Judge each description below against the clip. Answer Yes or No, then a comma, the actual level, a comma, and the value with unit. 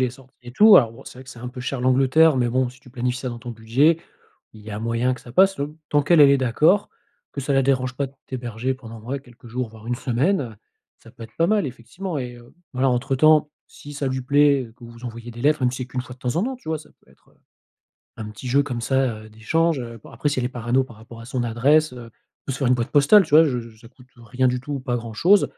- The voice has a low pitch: Yes, low, 125 Hz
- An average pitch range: Yes, average, 3.1 semitones